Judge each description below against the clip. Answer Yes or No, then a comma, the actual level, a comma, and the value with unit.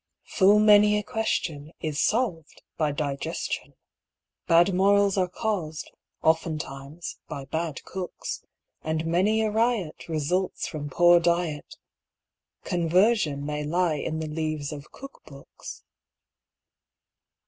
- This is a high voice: No, medium, 165 Hz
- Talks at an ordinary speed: No, slow, 115 wpm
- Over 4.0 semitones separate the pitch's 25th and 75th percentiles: Yes, average, 4.4 semitones